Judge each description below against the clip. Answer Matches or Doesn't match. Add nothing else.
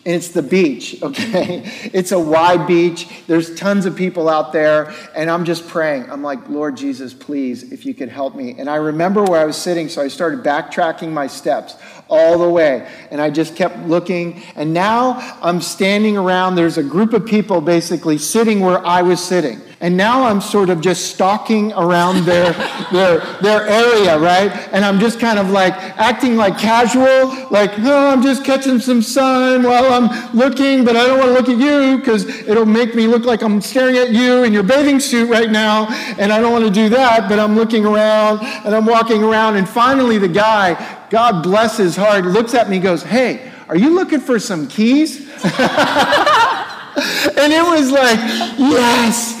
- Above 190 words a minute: Matches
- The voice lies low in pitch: Doesn't match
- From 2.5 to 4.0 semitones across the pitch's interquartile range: Doesn't match